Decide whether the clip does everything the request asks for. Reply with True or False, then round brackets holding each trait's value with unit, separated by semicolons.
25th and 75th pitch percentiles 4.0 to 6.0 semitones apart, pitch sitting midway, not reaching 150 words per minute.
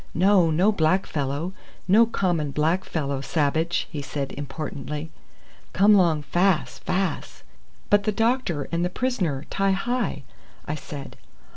True (4.8 semitones; 170 Hz; 140 wpm)